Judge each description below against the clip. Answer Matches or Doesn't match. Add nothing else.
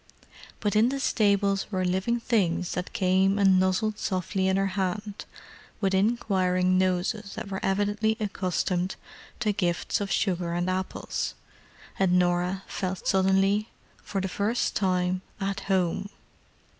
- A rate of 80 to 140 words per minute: Matches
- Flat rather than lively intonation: Matches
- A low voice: Doesn't match